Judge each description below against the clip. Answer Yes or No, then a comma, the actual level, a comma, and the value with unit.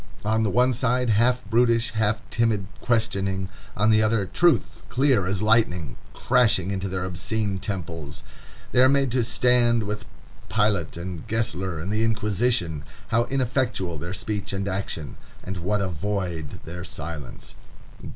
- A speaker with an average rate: Yes, average, 150 wpm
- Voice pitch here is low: Yes, low, 105 Hz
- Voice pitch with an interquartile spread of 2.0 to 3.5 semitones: No, average, 4.0 semitones